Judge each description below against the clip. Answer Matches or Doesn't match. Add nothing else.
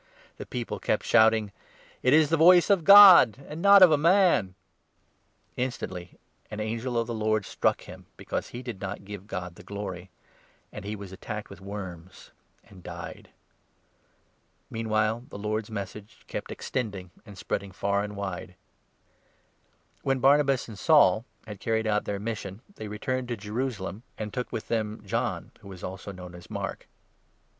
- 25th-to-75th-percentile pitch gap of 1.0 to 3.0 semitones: Doesn't match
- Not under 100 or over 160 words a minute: Doesn't match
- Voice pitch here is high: Doesn't match